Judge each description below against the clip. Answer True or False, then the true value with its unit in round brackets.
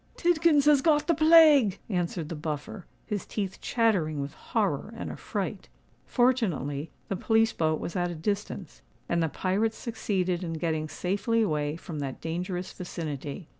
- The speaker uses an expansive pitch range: True (6.0 semitones)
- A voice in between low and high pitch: True (180 Hz)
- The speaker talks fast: False (155 wpm)